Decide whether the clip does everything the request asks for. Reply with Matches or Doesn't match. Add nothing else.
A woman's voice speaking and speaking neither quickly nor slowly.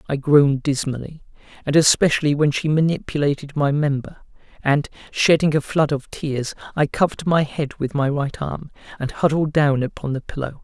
Doesn't match